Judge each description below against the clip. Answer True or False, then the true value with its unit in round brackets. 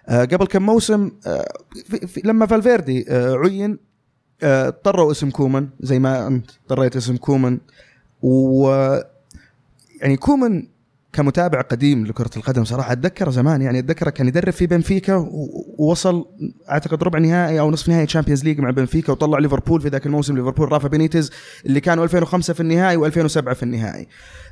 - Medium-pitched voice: True (145 Hz)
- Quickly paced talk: True (145 wpm)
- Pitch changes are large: False (4.5 semitones)